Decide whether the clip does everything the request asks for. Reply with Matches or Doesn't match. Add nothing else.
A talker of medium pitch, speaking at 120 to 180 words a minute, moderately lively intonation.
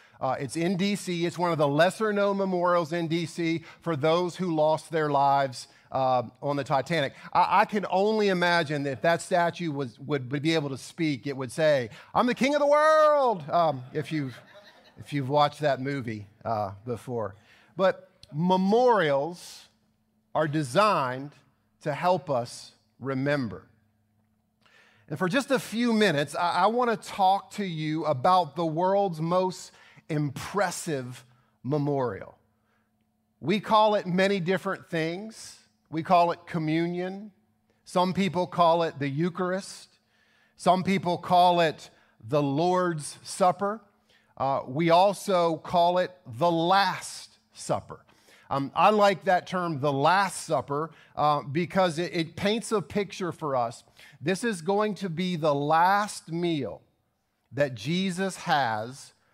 Matches